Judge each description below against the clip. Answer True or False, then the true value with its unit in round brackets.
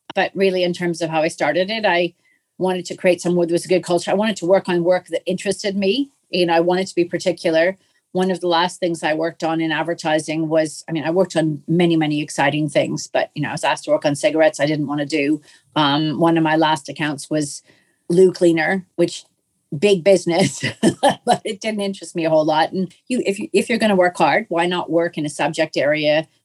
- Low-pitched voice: False (170 Hz)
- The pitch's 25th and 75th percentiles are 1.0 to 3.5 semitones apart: True (2.8 semitones)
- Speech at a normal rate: False (230 wpm)